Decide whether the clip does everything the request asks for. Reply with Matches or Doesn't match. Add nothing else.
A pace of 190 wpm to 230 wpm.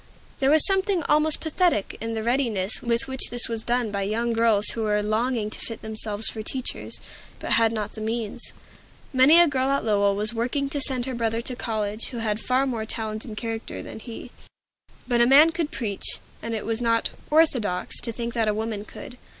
Matches